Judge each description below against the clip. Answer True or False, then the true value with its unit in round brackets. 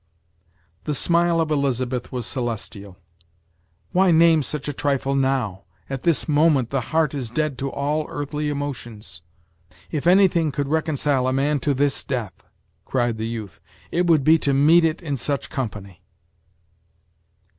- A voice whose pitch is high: False (140 Hz)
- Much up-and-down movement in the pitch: False (3.7 semitones)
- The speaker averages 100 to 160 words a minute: True (150 wpm)